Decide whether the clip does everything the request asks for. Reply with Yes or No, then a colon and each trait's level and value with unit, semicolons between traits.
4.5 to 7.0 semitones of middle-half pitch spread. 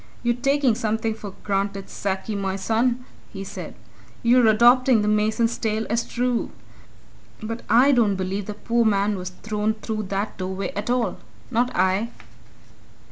No: average, 3.0 semitones